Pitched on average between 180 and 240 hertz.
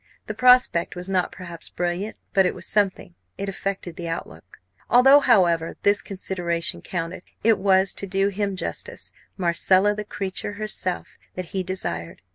Yes: high, 190 Hz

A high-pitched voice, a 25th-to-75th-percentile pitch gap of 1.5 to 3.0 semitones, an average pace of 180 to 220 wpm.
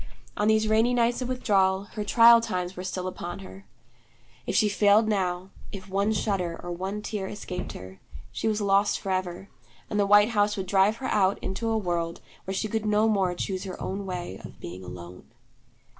Yes: high, 195 Hz; average, 2.7 semitones; average, 195 wpm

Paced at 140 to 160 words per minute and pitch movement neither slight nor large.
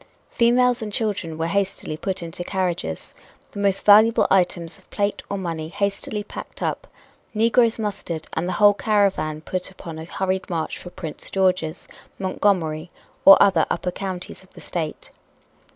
Yes: average, 155 wpm; average, 3.5 semitones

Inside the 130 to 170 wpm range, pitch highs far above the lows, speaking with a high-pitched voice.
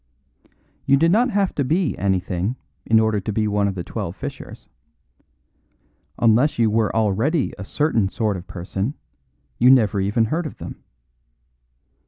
No: average, 155 wpm; wide, 5.9 semitones; low, 110 Hz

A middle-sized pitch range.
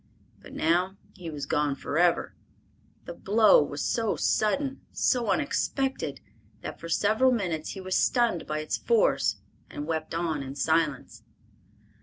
No: wide, 6.6 semitones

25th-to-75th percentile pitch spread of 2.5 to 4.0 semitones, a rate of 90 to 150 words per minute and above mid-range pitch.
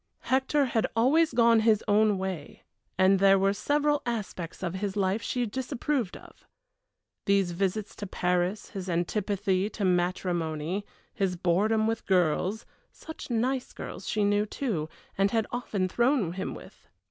Yes: average, 3.7 semitones; average, 145 wpm; high, 205 Hz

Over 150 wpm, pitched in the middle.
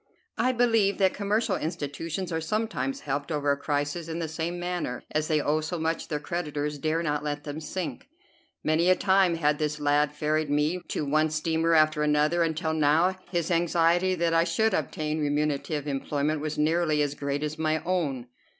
Yes: average, 185 wpm; medium, 155 Hz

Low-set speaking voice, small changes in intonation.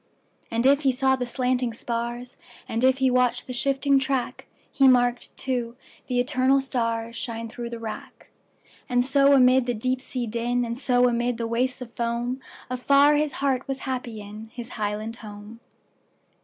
No: high, 245 Hz; narrow, 2.0 semitones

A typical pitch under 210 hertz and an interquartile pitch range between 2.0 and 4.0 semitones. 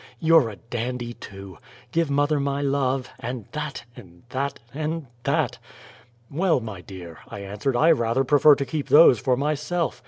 No: low, 135 Hz; average, 4.6 semitones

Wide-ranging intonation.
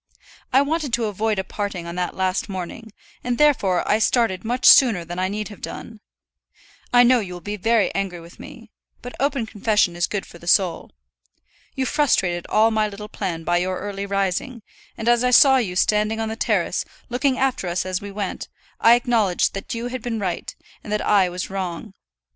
No: average, 4.3 semitones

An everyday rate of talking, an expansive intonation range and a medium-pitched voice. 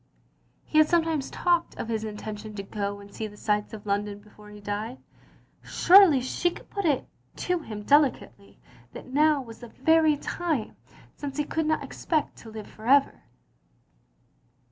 No: average, 165 wpm; wide, 6.8 semitones; high, 245 Hz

